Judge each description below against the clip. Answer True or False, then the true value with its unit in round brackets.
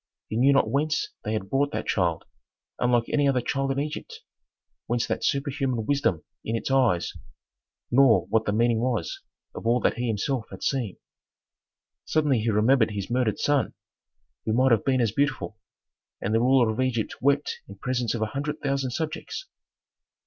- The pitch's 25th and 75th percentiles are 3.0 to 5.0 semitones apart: True (3.8 semitones)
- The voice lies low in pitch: True (125 Hz)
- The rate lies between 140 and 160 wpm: False (175 wpm)